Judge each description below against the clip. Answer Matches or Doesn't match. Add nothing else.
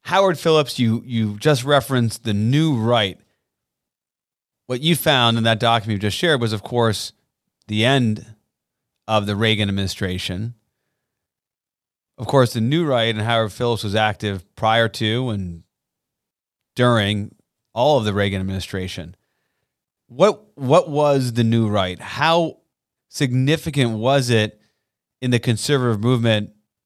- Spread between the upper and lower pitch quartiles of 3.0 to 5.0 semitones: Matches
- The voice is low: Matches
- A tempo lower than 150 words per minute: Matches